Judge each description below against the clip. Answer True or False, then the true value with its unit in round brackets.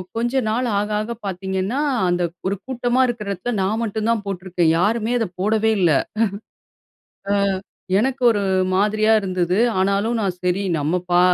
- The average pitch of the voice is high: True (205 Hz)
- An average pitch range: True (3.5 semitones)